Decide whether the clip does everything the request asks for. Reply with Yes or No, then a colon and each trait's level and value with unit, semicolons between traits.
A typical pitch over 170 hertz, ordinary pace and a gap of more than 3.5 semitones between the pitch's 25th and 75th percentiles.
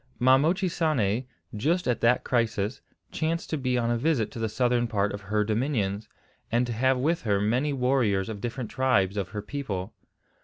No: low, 120 Hz; average, 185 wpm; average, 4.1 semitones